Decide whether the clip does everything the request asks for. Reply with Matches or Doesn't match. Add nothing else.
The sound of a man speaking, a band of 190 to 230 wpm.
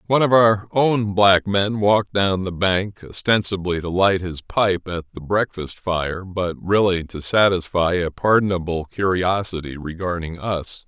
Doesn't match